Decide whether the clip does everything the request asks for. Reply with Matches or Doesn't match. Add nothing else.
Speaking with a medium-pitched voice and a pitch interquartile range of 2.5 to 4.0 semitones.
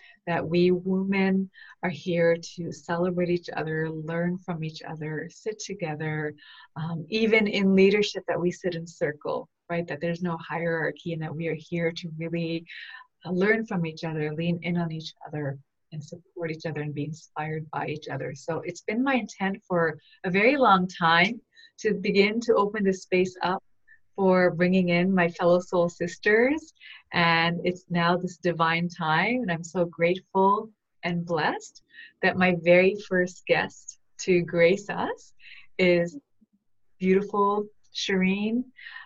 Matches